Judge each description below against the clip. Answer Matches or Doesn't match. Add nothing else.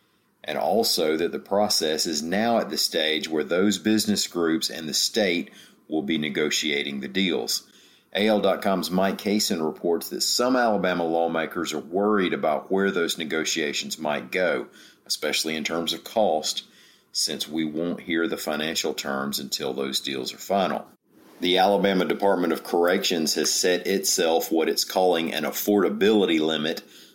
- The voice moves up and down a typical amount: Matches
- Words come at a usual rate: Matches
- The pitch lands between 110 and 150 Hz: Doesn't match